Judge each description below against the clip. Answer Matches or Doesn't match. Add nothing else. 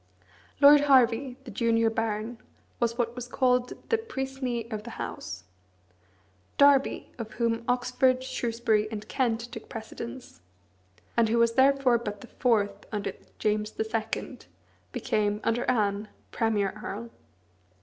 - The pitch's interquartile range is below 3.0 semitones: Matches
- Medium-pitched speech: Doesn't match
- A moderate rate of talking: Doesn't match